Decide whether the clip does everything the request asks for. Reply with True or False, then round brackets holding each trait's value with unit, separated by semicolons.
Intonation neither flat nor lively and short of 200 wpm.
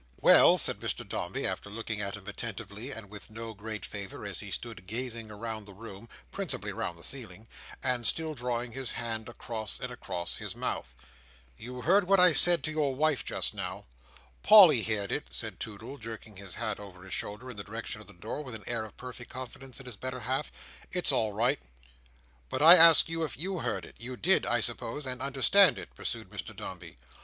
False (4.1 semitones; 205 wpm)